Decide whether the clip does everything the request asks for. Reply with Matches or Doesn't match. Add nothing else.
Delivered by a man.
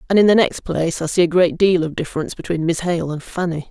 Doesn't match